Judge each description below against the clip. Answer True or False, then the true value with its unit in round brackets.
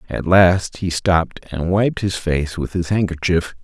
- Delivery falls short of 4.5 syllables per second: True (4.2 syllables/s)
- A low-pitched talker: True (90 Hz)